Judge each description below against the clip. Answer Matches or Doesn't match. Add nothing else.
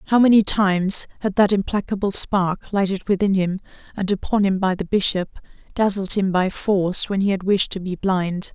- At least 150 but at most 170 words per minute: Doesn't match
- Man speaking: Doesn't match